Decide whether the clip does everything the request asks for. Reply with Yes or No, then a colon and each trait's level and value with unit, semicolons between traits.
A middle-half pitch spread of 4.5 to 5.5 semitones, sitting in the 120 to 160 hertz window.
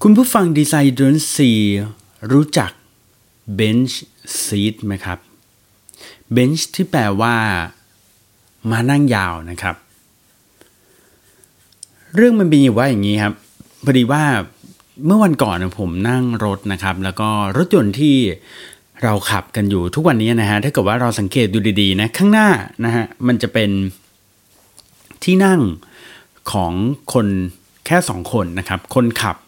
No: average, 5.1 semitones; low, 110 Hz